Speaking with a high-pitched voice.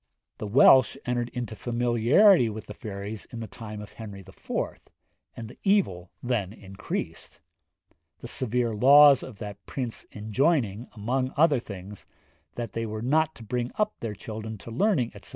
No: low, 115 Hz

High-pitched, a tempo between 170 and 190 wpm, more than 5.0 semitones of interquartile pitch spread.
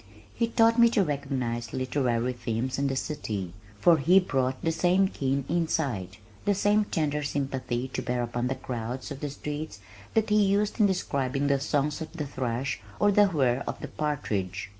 No: medium, 140 Hz; average, 180 wpm; wide, 5.5 semitones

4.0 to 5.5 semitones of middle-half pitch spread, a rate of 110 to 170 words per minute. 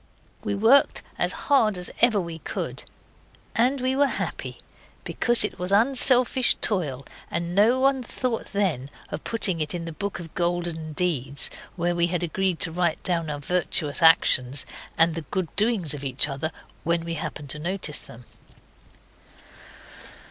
Yes: average, 5.1 semitones; average, 160 wpm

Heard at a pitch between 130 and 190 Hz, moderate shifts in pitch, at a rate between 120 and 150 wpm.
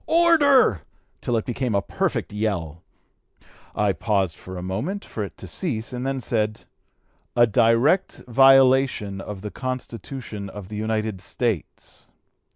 No: low, 110 Hz; average, 4.7 semitones; slow, 135 wpm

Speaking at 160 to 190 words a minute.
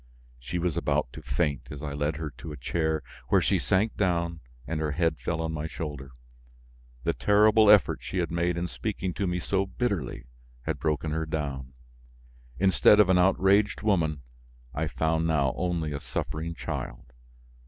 Yes: average, 175 wpm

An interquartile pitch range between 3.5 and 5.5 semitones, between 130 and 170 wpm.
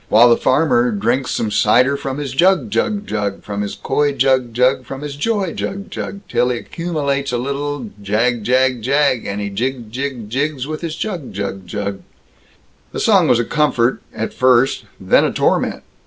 No: average, 4.1 semitones; average, 185 wpm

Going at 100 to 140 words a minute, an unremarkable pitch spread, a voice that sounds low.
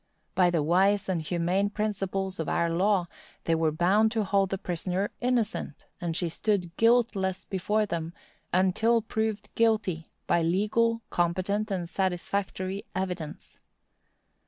No: slow, 135 wpm; average, 3.3 semitones; high, 190 Hz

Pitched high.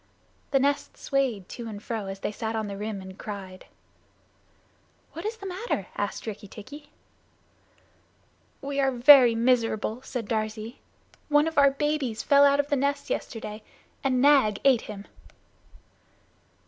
Yes: high, 240 Hz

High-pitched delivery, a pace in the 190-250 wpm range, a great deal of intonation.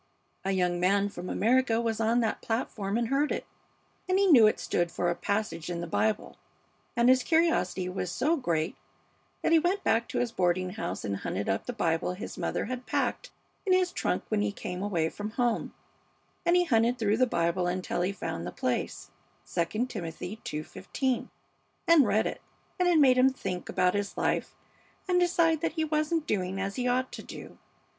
Yes: high, 220 Hz; average, 195 wpm; wide, 6.4 semitones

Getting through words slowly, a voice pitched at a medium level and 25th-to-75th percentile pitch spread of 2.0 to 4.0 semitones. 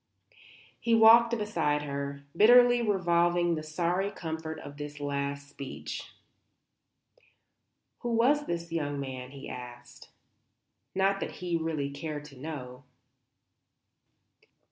No: slow, 110 wpm; medium, 160 Hz; wide, 5.5 semitones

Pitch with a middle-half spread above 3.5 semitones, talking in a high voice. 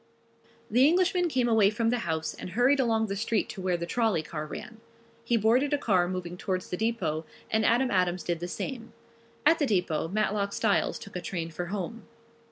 Yes: average, 4.9 semitones; high, 210 Hz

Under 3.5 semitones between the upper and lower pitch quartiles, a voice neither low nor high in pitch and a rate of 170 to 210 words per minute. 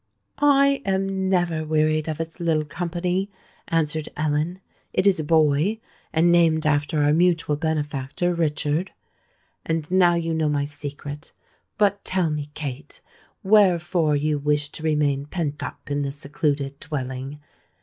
No: average, 2.9 semitones; medium, 155 Hz; average, 140 wpm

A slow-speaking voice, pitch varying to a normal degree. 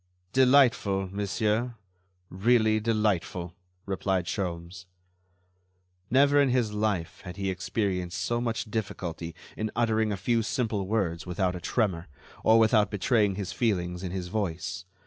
Yes: slow, 130 wpm; average, 3.7 semitones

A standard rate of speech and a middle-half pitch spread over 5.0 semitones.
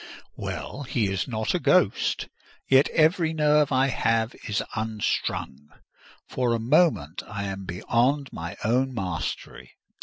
No: slow, 130 wpm; wide, 5.5 semitones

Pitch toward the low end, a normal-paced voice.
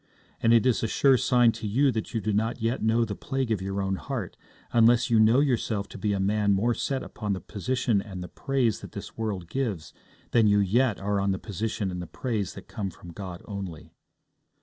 No: low, 110 Hz; fast, 225 wpm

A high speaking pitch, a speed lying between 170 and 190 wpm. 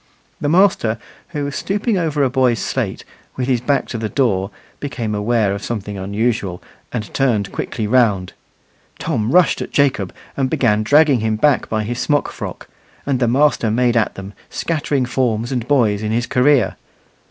No: low, 120 Hz; average, 175 wpm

